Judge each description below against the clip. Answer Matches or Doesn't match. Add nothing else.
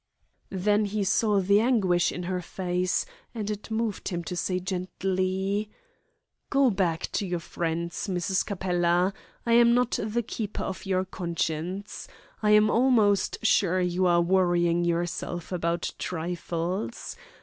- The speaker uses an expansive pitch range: Doesn't match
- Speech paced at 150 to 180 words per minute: Doesn't match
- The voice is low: Doesn't match